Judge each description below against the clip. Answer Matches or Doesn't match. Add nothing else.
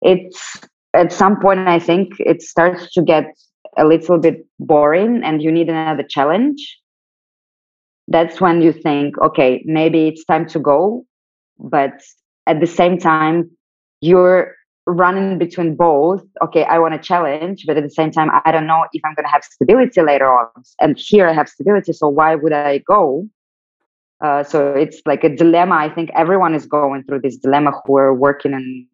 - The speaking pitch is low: Doesn't match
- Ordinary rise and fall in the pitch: Matches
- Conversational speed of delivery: Matches